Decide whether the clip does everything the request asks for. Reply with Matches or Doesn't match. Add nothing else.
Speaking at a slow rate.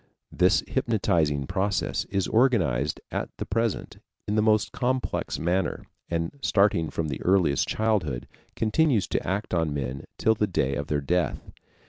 Doesn't match